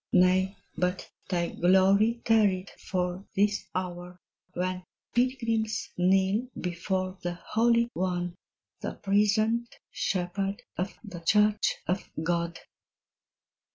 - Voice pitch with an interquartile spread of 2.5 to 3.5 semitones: Yes, average, 2.8 semitones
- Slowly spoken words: Yes, slow, 100 wpm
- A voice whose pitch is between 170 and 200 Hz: Yes, high, 190 Hz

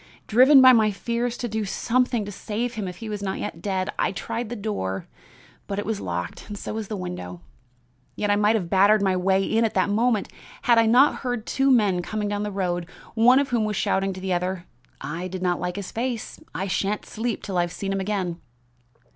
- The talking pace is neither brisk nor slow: No, fast, 220 wpm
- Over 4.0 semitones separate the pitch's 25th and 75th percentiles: No, average, 3.4 semitones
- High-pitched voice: Yes, high, 205 Hz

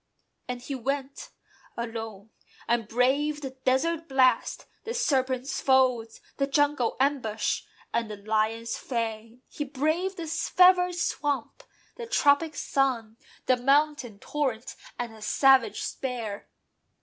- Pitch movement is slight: No, average, 4.1 semitones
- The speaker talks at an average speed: No, slow, 120 wpm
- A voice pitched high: Yes, very high, 260 Hz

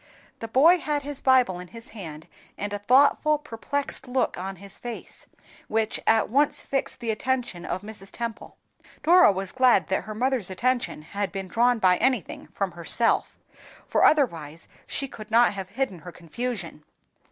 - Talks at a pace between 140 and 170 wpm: Yes, average, 165 wpm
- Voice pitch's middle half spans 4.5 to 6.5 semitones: Yes, average, 5.3 semitones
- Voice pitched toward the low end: No, high, 225 Hz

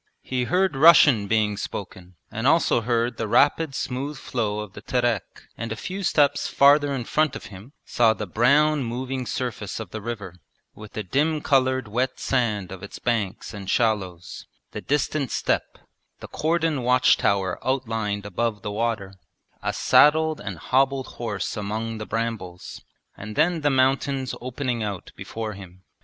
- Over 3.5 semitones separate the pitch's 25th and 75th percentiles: Yes, average, 4.6 semitones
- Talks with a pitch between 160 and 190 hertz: No, low, 120 Hz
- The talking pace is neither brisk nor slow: Yes, average, 160 wpm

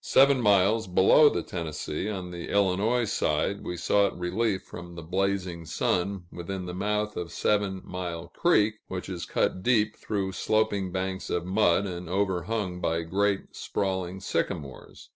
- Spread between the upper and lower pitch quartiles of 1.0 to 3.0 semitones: Yes, narrow, 2.6 semitones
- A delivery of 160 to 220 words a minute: No, average, 150 wpm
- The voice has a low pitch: Yes, very low, 95 Hz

